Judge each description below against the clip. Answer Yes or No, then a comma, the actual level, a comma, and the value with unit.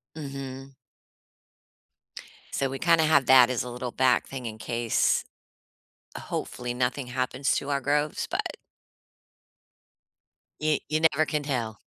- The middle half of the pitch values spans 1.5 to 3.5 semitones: Yes, average, 2.8 semitones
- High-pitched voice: No, low, 135 Hz